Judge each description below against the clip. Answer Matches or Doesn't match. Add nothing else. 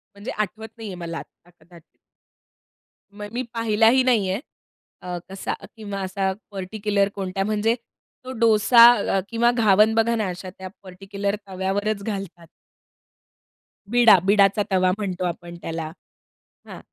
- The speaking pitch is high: Matches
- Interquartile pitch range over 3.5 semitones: Doesn't match